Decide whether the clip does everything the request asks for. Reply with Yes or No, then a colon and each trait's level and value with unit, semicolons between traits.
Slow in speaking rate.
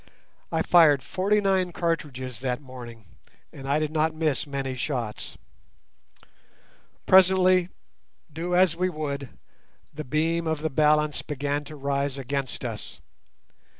Yes: slow, 125 wpm